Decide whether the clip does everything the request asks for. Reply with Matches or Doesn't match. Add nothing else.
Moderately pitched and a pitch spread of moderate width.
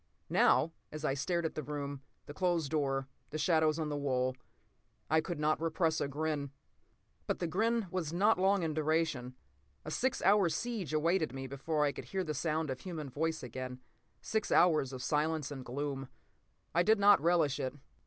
Matches